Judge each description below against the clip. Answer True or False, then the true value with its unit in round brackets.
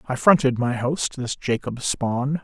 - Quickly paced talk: False (175 wpm)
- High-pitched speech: False (130 Hz)